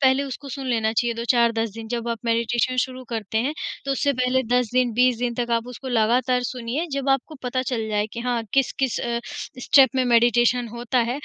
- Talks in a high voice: Yes, high, 245 Hz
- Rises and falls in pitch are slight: Yes, narrow, 1.7 semitones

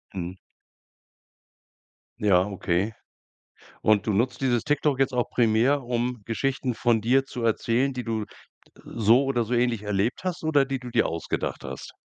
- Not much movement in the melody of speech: No, average, 3.5 semitones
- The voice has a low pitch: Yes, low, 120 Hz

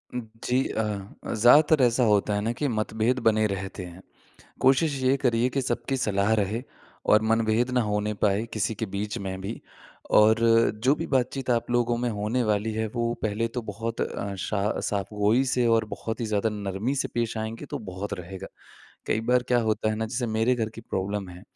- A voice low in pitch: Yes, low, 110 Hz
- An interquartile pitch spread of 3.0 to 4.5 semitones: No, narrow, 2.6 semitones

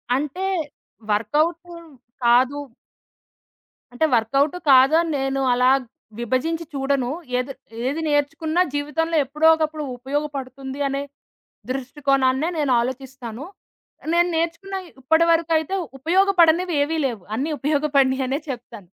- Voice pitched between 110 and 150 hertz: No, very high, 285 Hz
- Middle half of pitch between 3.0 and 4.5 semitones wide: Yes, average, 3.6 semitones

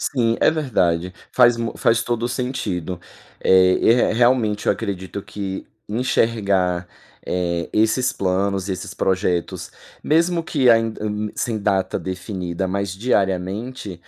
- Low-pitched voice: Yes, low, 105 Hz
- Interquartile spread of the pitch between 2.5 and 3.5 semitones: No, average, 4.1 semitones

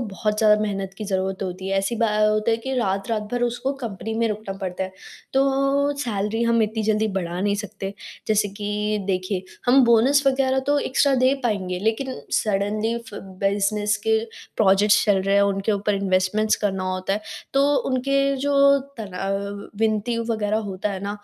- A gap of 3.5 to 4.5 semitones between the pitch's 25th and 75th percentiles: No, average, 2.9 semitones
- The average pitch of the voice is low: No, high, 210 Hz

